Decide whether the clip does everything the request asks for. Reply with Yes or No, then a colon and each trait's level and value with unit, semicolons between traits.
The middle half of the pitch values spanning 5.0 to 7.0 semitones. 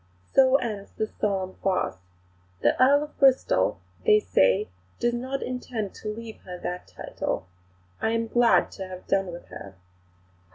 Yes: average, 5.3 semitones